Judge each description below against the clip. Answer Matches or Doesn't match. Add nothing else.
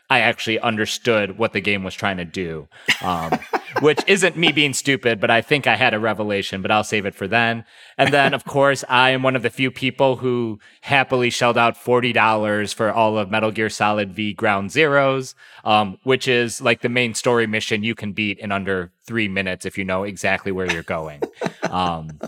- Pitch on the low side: Matches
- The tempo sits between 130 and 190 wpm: Doesn't match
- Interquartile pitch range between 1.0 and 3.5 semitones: Doesn't match